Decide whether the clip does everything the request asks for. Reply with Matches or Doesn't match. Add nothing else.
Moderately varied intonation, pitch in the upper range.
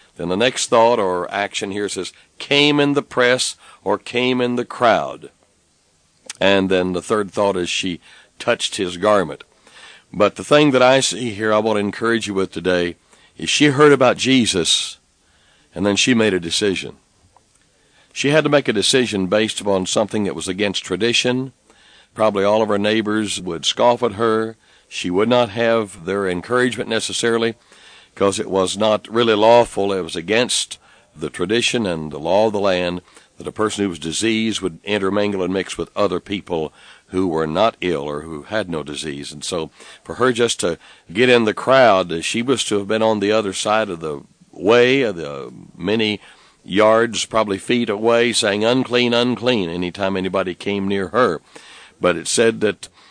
Doesn't match